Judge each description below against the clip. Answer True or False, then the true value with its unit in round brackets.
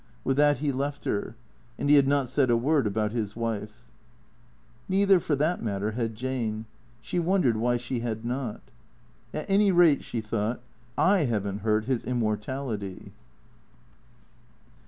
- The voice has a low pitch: True (120 Hz)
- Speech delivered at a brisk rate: False (160 wpm)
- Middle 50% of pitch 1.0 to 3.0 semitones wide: False (4.7 semitones)